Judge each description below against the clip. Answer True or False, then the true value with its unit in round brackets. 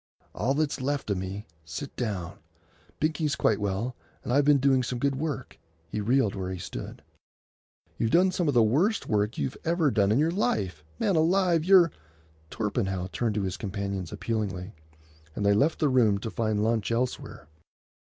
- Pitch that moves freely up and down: True (6.3 semitones)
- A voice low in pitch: True (115 Hz)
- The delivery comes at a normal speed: True (175 wpm)